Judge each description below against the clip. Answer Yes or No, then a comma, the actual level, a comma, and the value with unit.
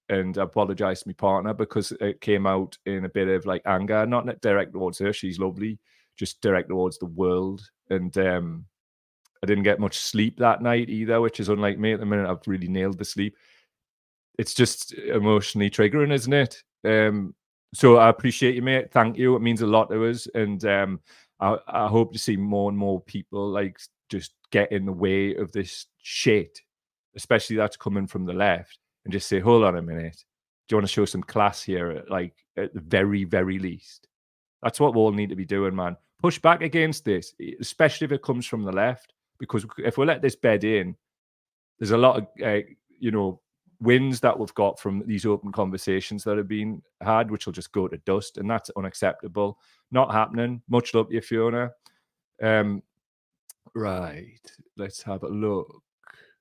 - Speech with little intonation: No, average, 3.0 semitones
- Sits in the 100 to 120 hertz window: Yes, low, 105 Hz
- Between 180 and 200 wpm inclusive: Yes, average, 195 wpm